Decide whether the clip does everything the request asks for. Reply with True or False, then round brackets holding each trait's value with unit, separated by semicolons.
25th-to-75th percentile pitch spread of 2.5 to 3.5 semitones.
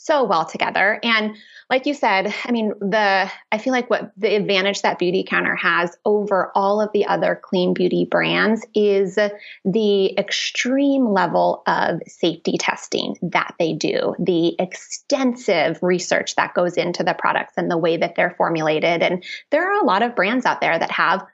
True (3.2 semitones)